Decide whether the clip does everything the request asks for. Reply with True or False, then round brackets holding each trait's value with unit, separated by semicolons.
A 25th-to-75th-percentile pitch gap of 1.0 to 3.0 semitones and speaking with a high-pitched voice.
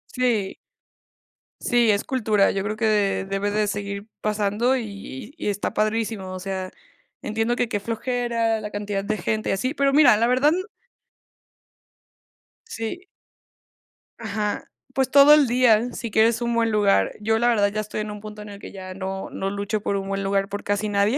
True (2.7 semitones; 215 Hz)